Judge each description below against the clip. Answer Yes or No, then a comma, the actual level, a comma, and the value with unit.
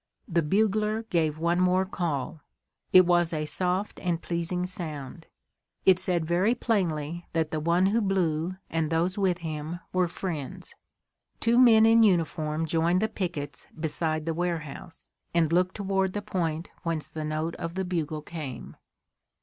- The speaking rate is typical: Yes, average, 155 wpm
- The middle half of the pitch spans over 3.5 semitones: No, average, 2.9 semitones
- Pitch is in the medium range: Yes, medium, 170 Hz